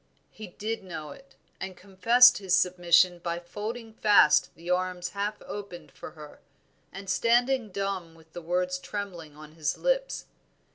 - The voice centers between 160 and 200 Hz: Yes, medium, 185 Hz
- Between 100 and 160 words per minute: Yes, average, 150 wpm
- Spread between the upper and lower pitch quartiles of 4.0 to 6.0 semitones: No, average, 3.5 semitones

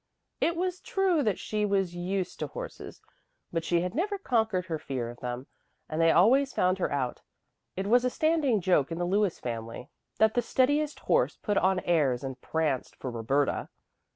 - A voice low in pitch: No, medium, 185 Hz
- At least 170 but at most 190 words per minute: Yes, average, 185 wpm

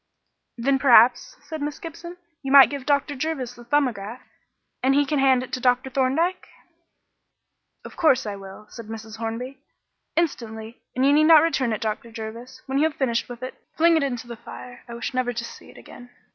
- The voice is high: Yes, very high, 255 Hz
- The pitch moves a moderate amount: Yes, average, 3.5 semitones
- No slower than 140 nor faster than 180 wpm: No, average, 200 wpm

